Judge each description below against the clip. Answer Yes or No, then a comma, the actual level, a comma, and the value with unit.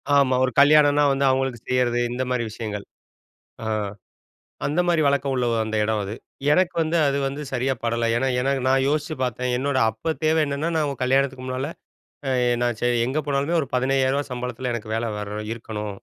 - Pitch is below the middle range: Yes, low, 130 Hz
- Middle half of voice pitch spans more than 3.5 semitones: No, average, 2.8 semitones